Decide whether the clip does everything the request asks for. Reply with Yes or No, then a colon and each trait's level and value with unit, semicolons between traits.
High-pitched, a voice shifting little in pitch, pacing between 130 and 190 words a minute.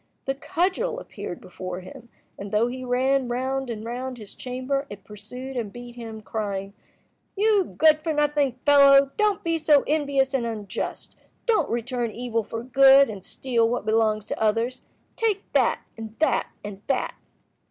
No: very high, 250 Hz; average, 3.9 semitones; average, 165 wpm